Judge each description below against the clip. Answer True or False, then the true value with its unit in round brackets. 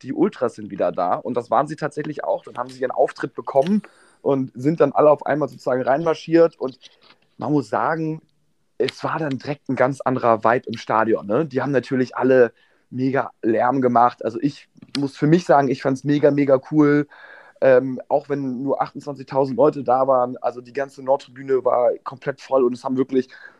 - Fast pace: True (200 wpm)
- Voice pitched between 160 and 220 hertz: False (135 Hz)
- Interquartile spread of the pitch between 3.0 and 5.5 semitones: False (2.4 semitones)